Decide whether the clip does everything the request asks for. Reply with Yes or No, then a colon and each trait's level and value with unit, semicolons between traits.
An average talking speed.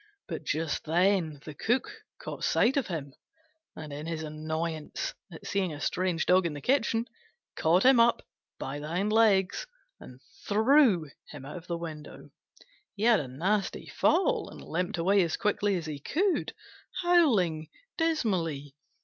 Yes: average, 160 wpm